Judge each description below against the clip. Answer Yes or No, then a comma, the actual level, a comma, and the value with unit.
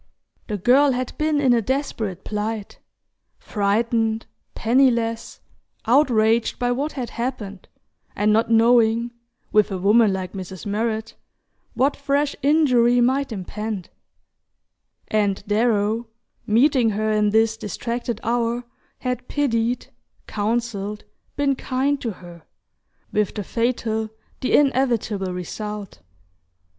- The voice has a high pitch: Yes, high, 230 Hz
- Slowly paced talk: Yes, slow, 110 wpm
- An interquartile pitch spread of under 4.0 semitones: Yes, average, 3.0 semitones